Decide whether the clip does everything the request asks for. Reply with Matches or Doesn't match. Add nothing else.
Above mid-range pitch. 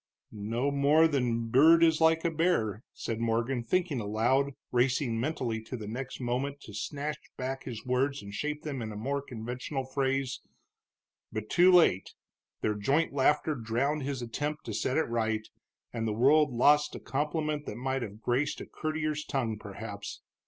Doesn't match